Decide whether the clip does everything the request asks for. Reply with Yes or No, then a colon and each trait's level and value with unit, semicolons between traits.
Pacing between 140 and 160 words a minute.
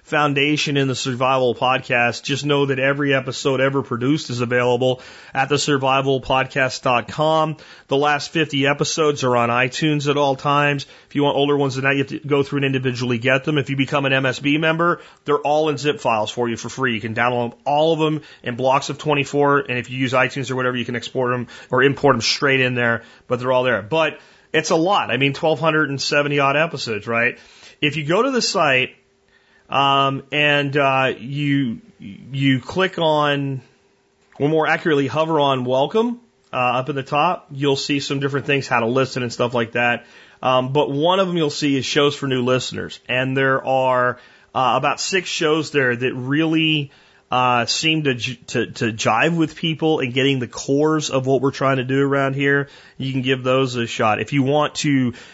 No: fast, 205 wpm